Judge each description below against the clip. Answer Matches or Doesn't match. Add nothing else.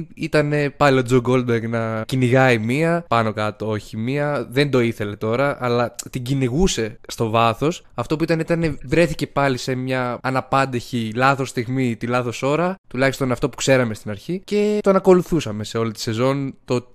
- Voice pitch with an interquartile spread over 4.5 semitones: Doesn't match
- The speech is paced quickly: Matches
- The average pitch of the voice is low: Matches